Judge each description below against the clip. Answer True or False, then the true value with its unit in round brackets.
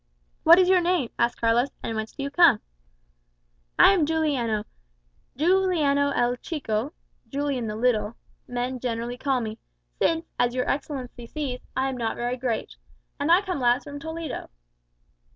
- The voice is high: True (260 Hz)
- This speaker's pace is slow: False (155 wpm)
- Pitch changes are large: False (4.5 semitones)